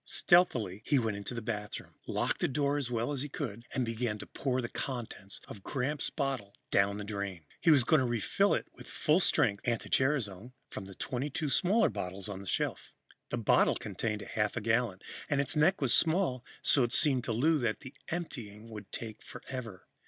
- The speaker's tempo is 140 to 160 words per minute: No, average, 200 wpm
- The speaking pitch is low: Yes, low, 120 Hz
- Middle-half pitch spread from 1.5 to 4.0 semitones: No, average, 5.2 semitones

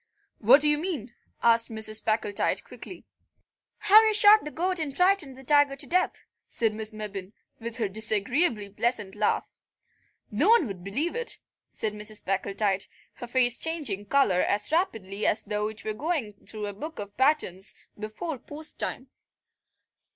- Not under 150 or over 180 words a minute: Yes, average, 160 wpm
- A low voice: No, high, 230 Hz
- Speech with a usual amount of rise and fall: No, wide, 6.6 semitones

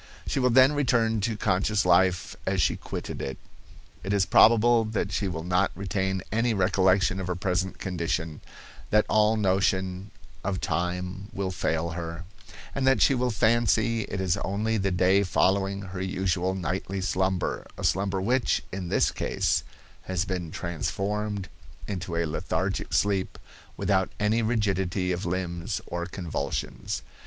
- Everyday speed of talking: Yes, average, 150 wpm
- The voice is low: Yes, very low, 95 Hz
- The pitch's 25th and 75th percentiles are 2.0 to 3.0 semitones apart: Yes, narrow, 2.6 semitones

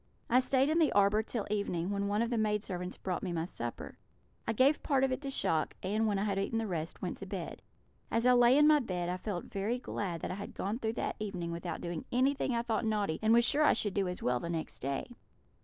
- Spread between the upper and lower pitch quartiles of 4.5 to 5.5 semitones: Yes, average, 4.9 semitones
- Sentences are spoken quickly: Yes, fast, 260 wpm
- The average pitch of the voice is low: No, high, 205 Hz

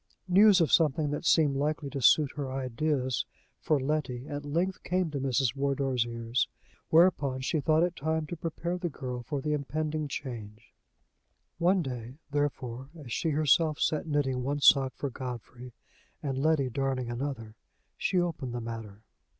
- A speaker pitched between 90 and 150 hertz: Yes, medium, 140 Hz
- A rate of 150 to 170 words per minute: Yes, average, 160 wpm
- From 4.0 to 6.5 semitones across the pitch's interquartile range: No, average, 3.5 semitones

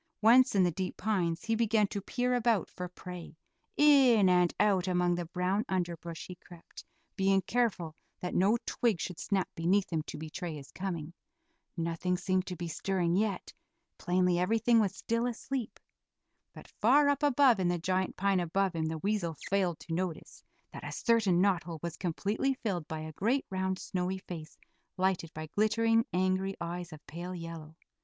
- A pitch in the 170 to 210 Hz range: Yes, medium, 185 Hz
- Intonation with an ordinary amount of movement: Yes, average, 3.6 semitones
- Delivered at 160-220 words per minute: Yes, average, 175 wpm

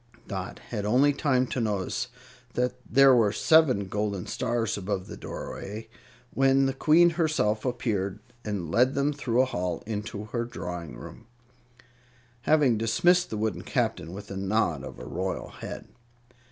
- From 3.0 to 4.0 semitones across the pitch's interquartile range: No, average, 4.8 semitones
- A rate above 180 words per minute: No, average, 155 wpm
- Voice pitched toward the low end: Yes, low, 110 Hz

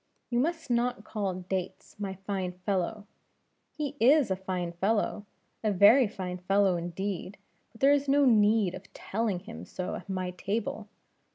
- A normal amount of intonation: Yes, average, 3.7 semitones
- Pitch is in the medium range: No, high, 200 Hz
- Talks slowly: No, average, 160 wpm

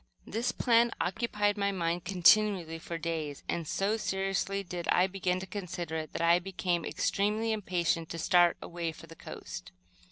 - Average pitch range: Yes, average, 3.0 semitones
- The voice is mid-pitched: Yes, medium, 180 Hz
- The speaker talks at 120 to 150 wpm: No, average, 165 wpm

